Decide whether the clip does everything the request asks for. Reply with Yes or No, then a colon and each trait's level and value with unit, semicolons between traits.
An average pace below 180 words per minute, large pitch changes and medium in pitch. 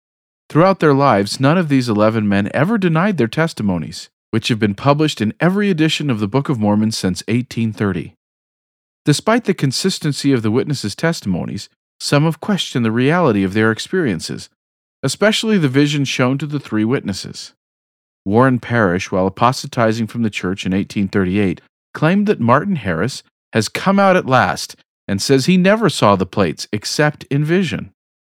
No: average, 165 wpm; wide, 6.9 semitones; low, 125 Hz